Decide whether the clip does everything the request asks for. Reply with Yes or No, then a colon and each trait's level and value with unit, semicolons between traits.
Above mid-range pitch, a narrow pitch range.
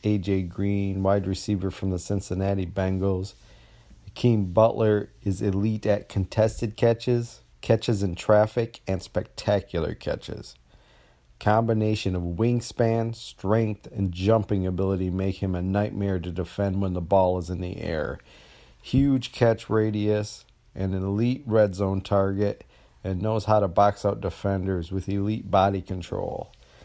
No: low, 100 Hz; narrow, 2.3 semitones